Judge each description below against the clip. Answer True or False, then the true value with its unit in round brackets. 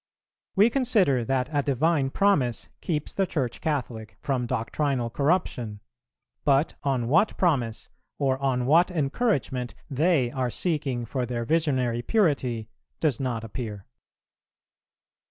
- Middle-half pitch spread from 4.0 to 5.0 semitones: True (4.6 semitones)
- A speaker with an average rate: False (120 wpm)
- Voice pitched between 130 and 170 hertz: True (135 Hz)